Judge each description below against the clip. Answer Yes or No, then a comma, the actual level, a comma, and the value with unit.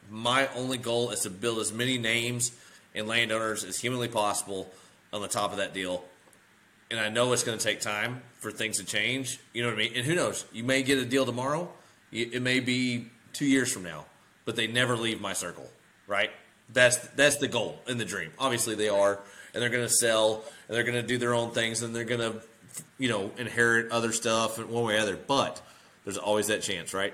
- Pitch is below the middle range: Yes, low, 115 Hz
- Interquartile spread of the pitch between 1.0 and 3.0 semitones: Yes, narrow, 2.4 semitones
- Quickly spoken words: Yes, fast, 220 wpm